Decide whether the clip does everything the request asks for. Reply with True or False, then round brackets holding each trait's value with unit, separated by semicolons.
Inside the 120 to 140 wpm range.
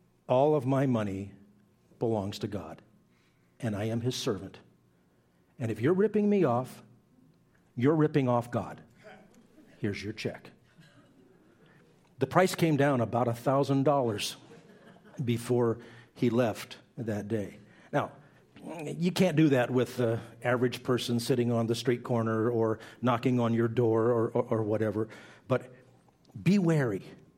True (135 wpm)